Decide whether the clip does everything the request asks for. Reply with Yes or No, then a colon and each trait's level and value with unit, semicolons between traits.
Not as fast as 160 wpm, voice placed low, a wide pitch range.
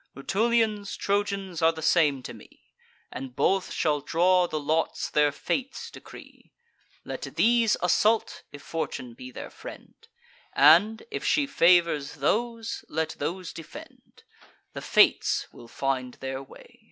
No: slow, 135 wpm; medium, 165 Hz; wide, 6.1 semitones